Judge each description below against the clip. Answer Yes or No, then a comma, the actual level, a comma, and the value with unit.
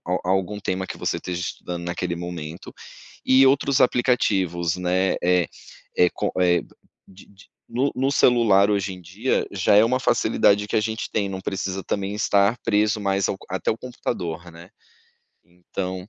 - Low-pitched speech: Yes, very low, 95 Hz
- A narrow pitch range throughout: No, average, 3.1 semitones